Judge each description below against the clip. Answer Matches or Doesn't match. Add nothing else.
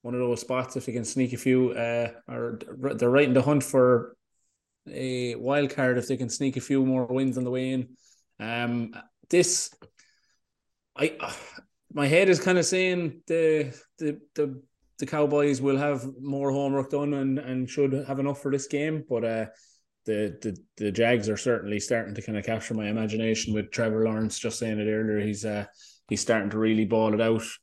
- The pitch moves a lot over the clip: Doesn't match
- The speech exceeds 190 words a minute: Matches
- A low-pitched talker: Matches